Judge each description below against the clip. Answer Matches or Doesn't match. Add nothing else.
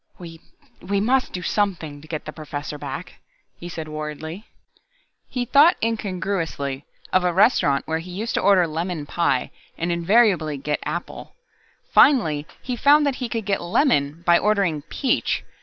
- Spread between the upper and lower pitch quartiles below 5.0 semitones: Doesn't match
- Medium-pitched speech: Matches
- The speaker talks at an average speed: Matches